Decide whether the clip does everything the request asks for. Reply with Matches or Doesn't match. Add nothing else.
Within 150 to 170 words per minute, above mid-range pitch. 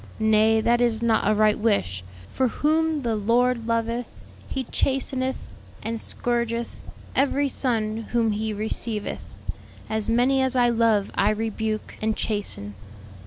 Doesn't match